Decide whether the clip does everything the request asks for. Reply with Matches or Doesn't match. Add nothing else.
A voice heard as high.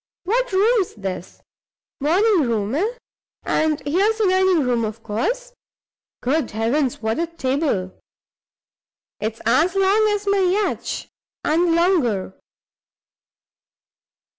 Matches